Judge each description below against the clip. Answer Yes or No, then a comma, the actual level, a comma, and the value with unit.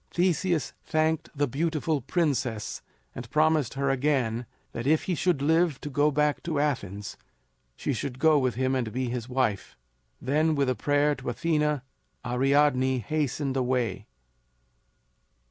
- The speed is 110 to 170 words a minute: Yes, average, 145 wpm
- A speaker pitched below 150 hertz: Yes, medium, 140 Hz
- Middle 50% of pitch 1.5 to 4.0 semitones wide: Yes, average, 3.3 semitones